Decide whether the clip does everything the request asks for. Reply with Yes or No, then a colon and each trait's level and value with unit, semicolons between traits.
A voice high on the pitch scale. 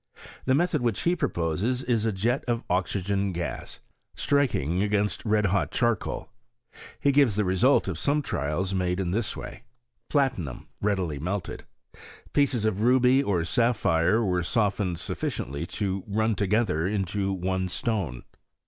No: low, 100 Hz